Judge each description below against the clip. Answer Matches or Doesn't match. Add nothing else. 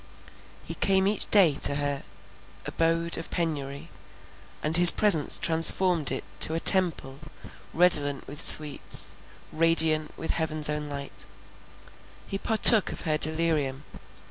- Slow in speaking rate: Matches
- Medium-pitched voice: Matches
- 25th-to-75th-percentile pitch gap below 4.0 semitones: Matches